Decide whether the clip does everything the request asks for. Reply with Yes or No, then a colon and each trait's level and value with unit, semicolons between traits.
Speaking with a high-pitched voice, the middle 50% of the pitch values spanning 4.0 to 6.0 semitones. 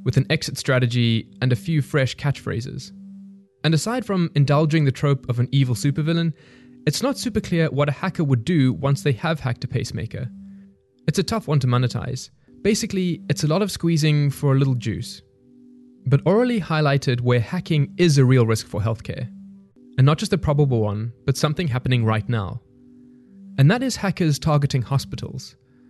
No: medium, 140 Hz; average, 4.9 semitones